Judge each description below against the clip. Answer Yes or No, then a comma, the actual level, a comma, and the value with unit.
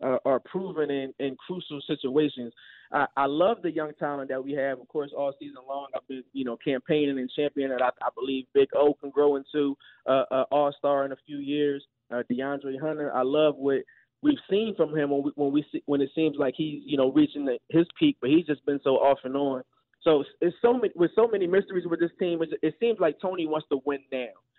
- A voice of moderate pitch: Yes, medium, 145 Hz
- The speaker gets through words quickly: Yes, fast, 245 wpm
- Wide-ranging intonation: No, average, 3.0 semitones